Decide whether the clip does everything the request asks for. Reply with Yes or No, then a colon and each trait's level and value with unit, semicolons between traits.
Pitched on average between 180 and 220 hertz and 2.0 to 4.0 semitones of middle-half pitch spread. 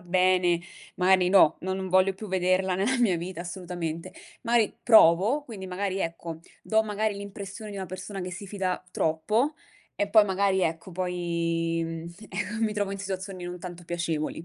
Yes: medium, 185 Hz; narrow, 2.4 semitones